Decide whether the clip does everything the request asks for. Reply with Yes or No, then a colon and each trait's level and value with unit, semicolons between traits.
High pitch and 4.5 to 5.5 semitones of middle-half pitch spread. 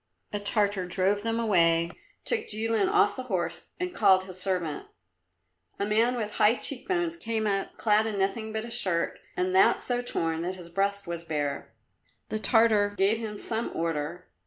No: high, 205 Hz; average, 3.9 semitones